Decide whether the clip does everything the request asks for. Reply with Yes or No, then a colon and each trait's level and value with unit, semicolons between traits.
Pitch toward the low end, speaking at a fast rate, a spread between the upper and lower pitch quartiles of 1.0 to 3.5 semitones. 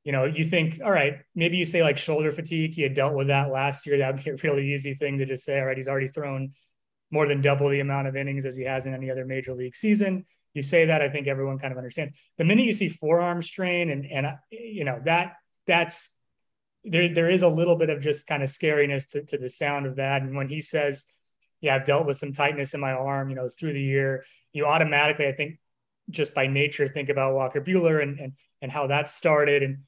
No: medium, 145 Hz; fast, 245 wpm; average, 2.8 semitones